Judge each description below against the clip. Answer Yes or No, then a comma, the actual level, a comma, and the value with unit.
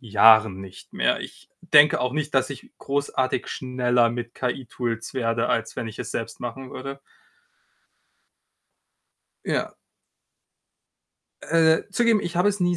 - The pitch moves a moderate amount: Yes, average, 4.7 semitones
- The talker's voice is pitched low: Yes, low, 130 Hz